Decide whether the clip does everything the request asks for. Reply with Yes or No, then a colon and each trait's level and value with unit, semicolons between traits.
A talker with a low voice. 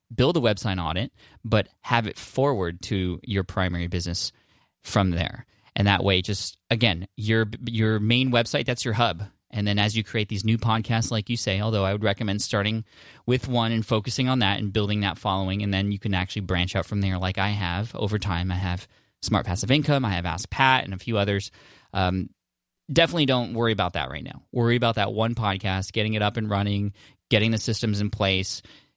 Yes: low, 105 Hz